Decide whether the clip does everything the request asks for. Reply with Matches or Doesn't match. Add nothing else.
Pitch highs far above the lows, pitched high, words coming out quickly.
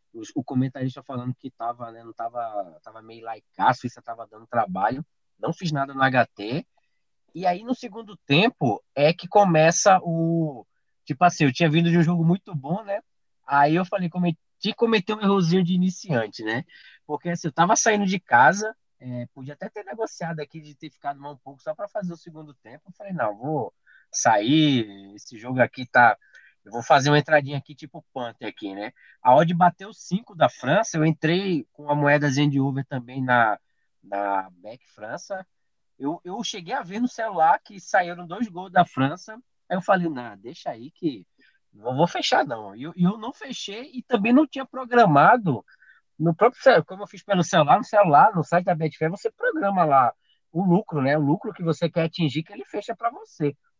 Doesn't match